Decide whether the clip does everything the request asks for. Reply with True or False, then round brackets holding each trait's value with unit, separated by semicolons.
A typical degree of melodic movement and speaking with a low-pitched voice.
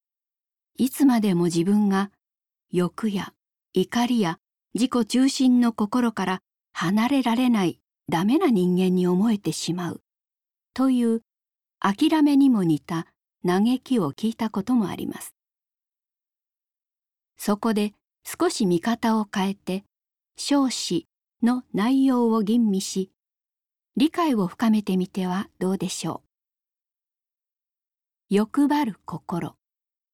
False (4.9 semitones; 215 Hz)